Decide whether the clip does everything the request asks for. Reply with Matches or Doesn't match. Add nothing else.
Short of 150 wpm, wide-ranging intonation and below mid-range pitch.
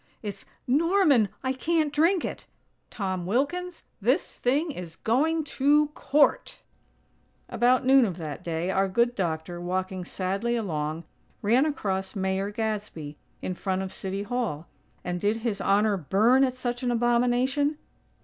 Doesn't match